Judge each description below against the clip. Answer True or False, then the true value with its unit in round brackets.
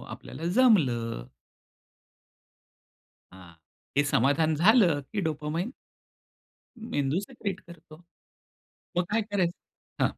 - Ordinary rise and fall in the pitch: False (5.9 semitones)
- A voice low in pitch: False (165 Hz)